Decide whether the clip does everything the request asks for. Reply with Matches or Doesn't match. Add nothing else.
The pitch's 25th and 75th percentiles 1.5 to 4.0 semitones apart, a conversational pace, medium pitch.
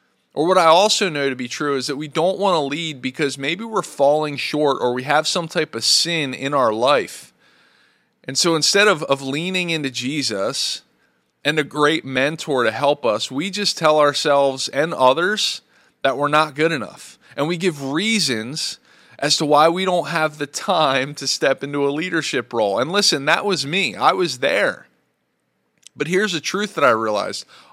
Matches